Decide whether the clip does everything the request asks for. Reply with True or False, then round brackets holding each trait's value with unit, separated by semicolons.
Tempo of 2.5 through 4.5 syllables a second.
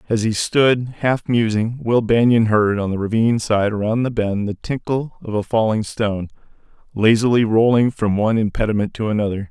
False (5.3 syllables/s)